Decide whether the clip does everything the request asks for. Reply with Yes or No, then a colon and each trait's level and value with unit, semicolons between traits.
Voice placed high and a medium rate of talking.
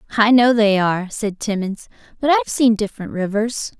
Yes: high, 215 Hz; average, 175 wpm